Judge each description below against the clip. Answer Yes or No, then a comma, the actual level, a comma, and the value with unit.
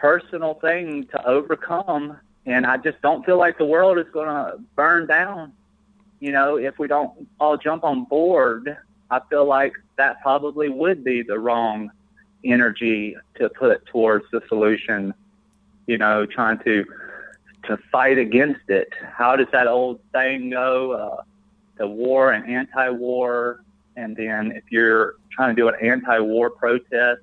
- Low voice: Yes, low, 130 Hz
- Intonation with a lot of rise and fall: No, average, 4.7 semitones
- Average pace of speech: Yes, average, 155 wpm